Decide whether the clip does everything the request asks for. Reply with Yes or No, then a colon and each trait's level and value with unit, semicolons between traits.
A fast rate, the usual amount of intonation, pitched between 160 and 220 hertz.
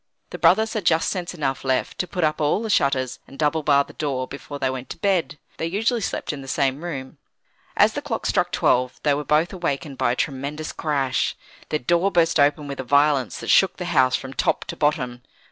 No: fast, 225 wpm; average, 4.0 semitones; medium, 145 Hz